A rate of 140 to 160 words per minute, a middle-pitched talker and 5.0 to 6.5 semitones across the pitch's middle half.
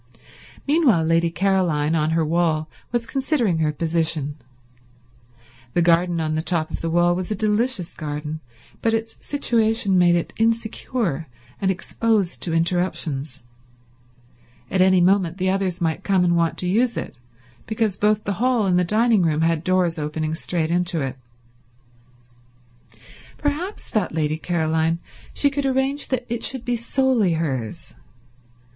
Yes: average, 150 wpm; medium, 180 Hz; wide, 5.5 semitones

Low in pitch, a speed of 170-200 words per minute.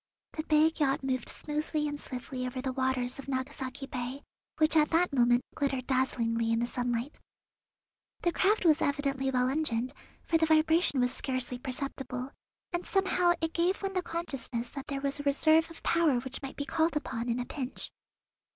No: very high, 275 Hz; average, 180 wpm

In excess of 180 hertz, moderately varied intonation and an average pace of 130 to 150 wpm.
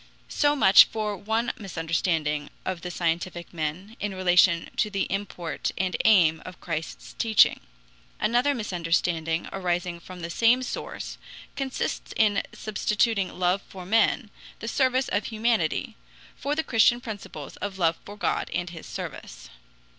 Yes: high, 190 Hz; average, 4.5 semitones; average, 140 wpm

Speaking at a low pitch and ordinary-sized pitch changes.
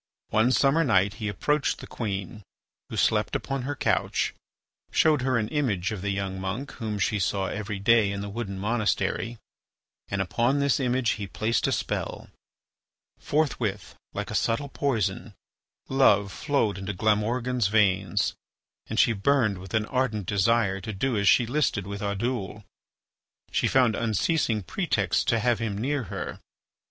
Yes: low, 110 Hz; average, 4.1 semitones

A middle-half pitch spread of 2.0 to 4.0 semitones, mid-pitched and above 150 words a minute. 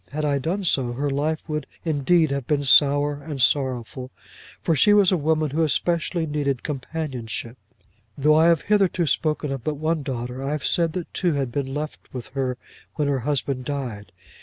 Yes: average, 3.0 semitones; medium, 145 Hz; average, 185 wpm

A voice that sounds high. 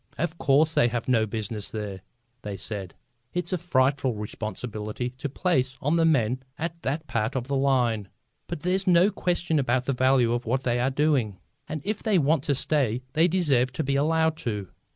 No: low, 135 Hz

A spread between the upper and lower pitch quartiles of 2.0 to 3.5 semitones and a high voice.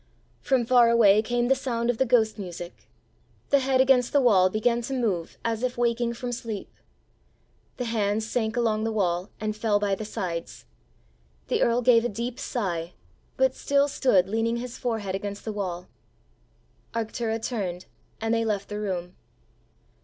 Yes: average, 3.1 semitones; high, 225 Hz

